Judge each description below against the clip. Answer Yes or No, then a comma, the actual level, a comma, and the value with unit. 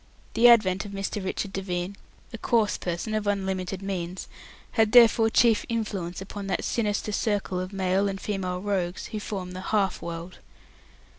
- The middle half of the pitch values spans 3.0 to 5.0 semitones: No, narrow, 2.4 semitones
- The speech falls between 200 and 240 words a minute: No, average, 160 wpm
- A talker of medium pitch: No, high, 195 Hz